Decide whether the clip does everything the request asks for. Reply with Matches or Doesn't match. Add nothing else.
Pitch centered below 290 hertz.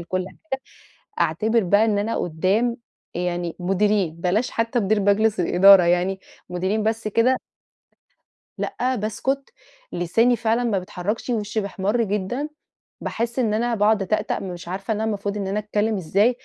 Matches